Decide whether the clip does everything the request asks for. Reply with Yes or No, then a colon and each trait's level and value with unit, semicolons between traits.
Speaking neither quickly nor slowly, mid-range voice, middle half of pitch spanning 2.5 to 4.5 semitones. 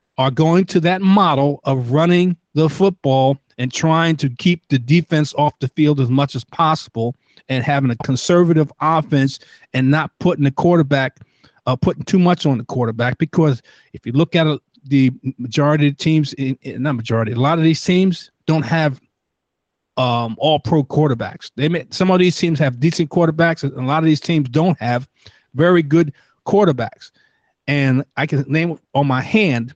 Yes: average, 180 wpm; medium, 150 Hz; average, 3.8 semitones